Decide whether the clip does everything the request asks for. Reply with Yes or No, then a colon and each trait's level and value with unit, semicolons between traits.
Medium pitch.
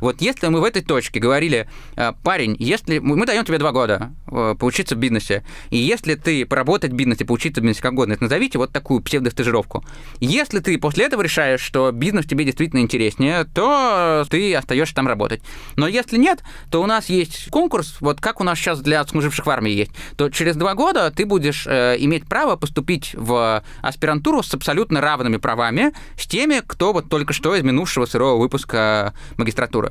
Yes: medium, 150 Hz